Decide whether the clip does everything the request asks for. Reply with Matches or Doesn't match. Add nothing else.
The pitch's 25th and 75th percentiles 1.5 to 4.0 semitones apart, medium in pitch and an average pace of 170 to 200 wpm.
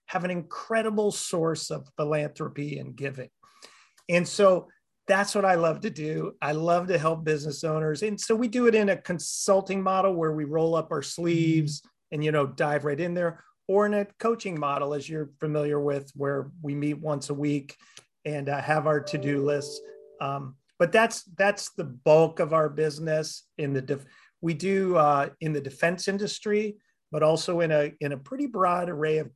Doesn't match